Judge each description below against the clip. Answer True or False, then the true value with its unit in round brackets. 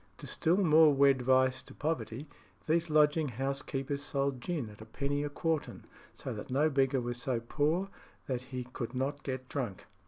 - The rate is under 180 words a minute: False (185 wpm)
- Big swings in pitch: False (2.8 semitones)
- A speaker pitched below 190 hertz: True (140 Hz)